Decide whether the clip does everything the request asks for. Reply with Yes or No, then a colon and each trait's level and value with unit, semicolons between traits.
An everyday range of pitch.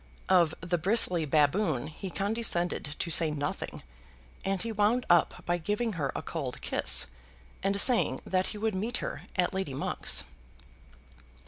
Yes: average, 4.5 semitones